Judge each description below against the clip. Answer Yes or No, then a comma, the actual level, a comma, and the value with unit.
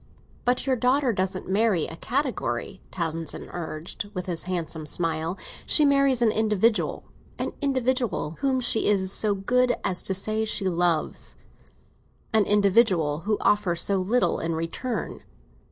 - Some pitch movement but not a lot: No, wide, 5.9 semitones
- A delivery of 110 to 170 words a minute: Yes, slow, 135 wpm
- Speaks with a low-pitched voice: No, high, 200 Hz